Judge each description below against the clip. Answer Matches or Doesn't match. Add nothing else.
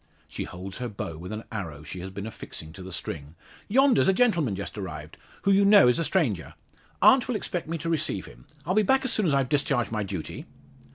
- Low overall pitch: Matches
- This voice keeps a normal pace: Doesn't match